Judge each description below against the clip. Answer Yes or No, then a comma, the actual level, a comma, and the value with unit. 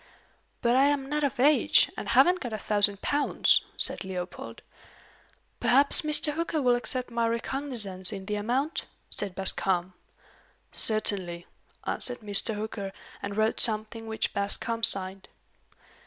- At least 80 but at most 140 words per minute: Yes, slow, 135 wpm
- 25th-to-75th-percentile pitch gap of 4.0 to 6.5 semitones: Yes, average, 5.1 semitones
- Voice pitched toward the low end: No, high, 220 Hz